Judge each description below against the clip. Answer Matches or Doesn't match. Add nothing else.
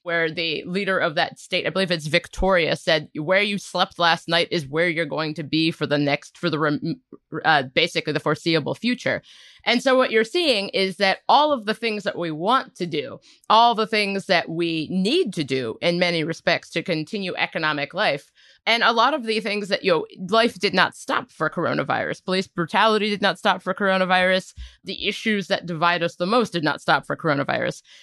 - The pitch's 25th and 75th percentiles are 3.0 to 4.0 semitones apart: Matches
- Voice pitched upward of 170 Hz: Matches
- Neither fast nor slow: Doesn't match